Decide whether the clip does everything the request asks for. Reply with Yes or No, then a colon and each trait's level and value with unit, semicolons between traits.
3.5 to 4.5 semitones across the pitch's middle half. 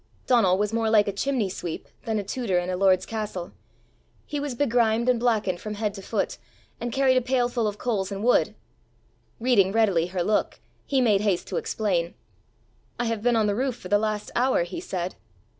Yes: average, 3.8 semitones